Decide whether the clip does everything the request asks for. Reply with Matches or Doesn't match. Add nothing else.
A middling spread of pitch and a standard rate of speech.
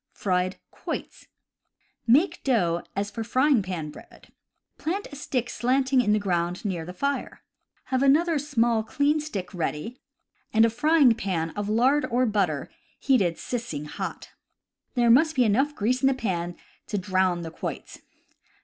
Doesn't match